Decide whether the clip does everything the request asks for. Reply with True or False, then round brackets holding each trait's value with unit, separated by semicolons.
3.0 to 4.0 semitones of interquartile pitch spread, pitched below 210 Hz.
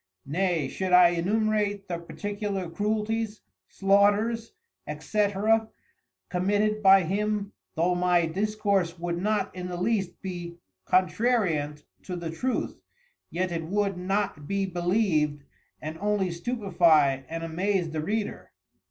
True (3.4 semitones; 190 Hz)